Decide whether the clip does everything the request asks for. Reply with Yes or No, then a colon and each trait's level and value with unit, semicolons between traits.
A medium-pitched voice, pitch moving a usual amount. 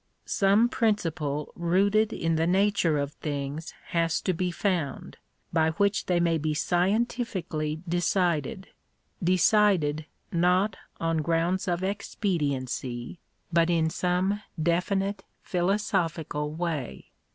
Yes: medium, 175 Hz; average, 3.5 semitones